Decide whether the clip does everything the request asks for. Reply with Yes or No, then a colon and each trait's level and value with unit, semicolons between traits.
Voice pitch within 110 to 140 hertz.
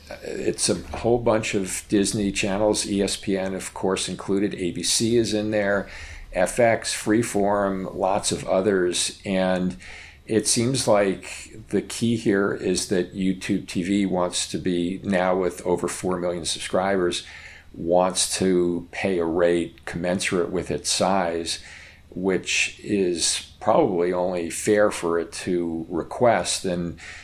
No: very low, 95 Hz